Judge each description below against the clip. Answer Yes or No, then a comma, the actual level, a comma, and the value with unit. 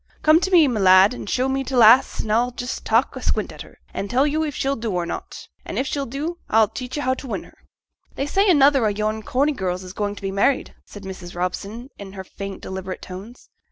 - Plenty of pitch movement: Yes, wide, 5.8 semitones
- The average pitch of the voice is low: No, high, 230 Hz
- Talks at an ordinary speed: No, fast, 250 wpm